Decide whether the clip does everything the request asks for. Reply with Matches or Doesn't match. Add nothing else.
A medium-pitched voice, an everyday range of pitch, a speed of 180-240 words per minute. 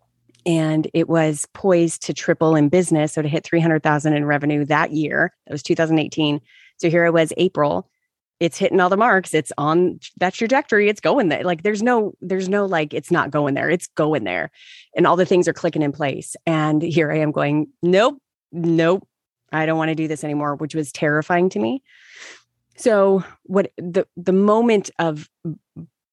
Matches